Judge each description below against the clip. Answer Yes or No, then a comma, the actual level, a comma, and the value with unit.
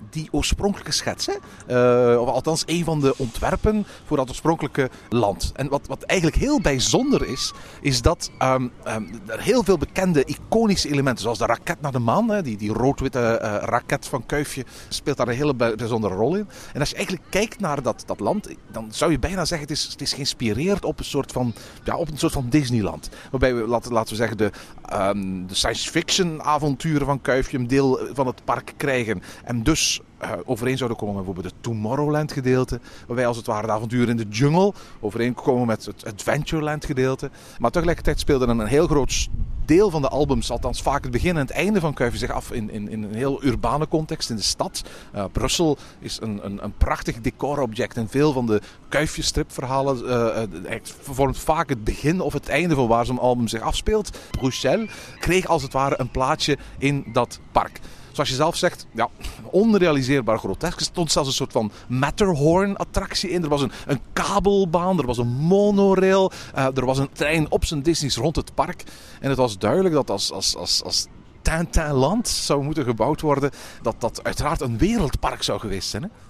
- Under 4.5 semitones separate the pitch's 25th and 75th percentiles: No, average, 5.0 semitones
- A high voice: No, low, 135 Hz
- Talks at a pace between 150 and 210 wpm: Yes, fast, 200 wpm